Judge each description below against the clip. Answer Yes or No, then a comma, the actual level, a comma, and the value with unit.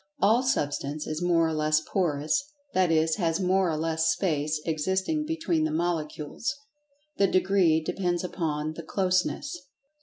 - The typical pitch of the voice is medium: Yes, medium, 175 Hz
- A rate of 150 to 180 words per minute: No, average, 140 wpm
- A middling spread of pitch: Yes, average, 3.9 semitones